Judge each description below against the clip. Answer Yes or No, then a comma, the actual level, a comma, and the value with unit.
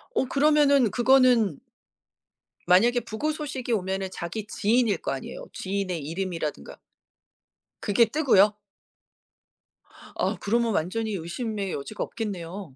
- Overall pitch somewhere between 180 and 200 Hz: No, high, 210 Hz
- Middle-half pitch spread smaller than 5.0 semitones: Yes, average, 4.6 semitones